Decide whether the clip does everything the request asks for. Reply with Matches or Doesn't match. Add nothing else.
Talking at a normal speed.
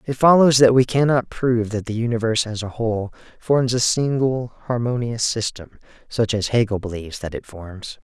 Matches